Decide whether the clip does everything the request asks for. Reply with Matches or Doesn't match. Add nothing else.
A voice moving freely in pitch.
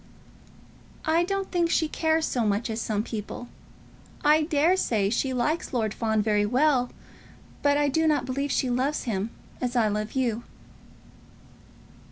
Matches